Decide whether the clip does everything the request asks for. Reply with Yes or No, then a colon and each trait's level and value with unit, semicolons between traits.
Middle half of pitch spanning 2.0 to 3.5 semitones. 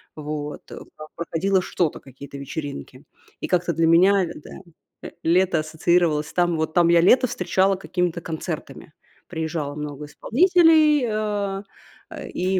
No: average, 3.9 semitones